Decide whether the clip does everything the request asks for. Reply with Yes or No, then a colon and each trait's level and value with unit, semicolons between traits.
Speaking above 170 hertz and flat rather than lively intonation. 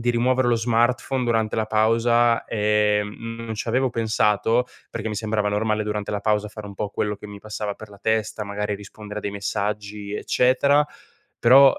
No: low, 110 Hz; narrow, 2.0 semitones